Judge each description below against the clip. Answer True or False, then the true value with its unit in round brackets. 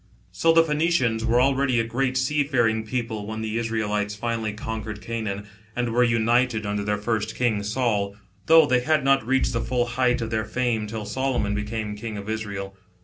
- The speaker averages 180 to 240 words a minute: True (185 wpm)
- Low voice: True (115 Hz)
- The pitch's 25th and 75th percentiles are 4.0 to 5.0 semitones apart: False (3.0 semitones)